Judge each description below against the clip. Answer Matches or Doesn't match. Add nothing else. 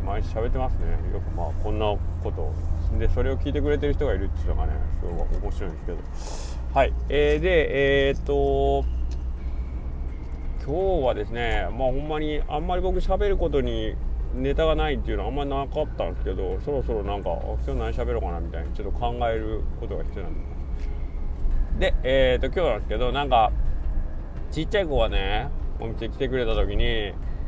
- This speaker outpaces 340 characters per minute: Matches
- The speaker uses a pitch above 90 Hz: Doesn't match